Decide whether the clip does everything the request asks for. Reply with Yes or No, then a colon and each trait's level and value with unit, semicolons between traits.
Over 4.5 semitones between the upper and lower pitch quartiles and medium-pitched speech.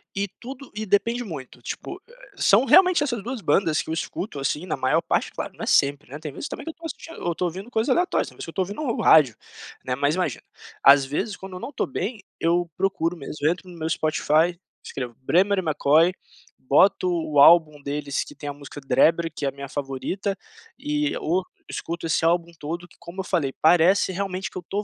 Yes: average, 5.1 semitones; medium, 175 Hz